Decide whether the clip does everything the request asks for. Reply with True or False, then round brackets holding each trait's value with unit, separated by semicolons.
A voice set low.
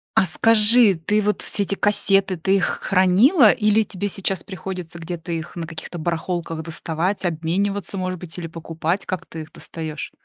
False (185 Hz)